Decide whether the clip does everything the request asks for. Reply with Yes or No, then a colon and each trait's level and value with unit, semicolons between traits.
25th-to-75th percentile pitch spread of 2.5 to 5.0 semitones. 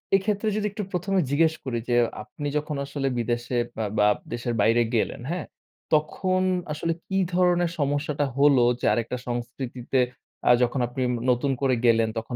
No: wide, 5.6 semitones